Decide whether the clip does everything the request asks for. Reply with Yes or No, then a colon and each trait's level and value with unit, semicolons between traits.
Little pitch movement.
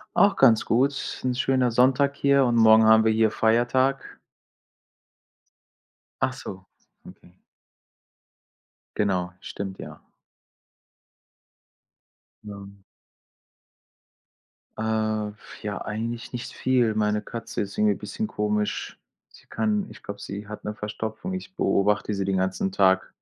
No: average, 3.6 semitones